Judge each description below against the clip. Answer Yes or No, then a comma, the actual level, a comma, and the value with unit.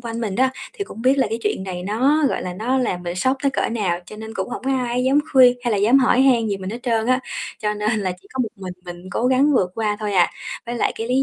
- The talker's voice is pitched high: Yes, high, 230 Hz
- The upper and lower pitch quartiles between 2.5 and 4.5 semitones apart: Yes, average, 4.0 semitones